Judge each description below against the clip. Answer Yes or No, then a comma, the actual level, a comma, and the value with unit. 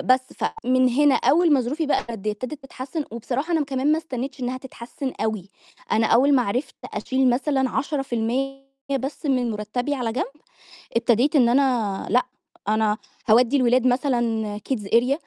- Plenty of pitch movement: No, average, 2.8 semitones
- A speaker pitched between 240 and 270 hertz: Yes, very high, 255 Hz